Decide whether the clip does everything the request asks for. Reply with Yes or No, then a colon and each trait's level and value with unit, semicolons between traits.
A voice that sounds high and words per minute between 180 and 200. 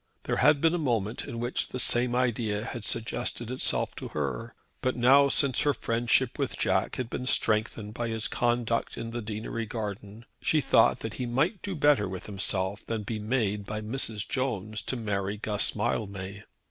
No: low, 115 Hz; average, 185 wpm